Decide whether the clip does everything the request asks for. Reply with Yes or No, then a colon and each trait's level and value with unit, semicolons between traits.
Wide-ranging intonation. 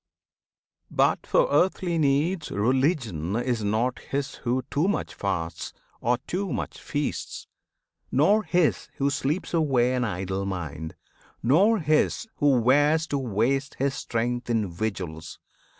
Yes: wide, 5.9 semitones